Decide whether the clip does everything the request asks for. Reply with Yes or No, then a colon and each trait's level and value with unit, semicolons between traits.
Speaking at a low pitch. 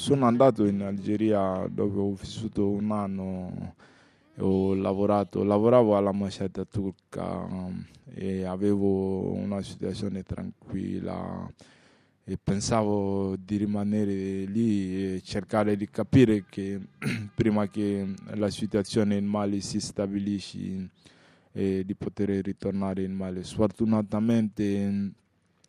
Yes: low, 100 Hz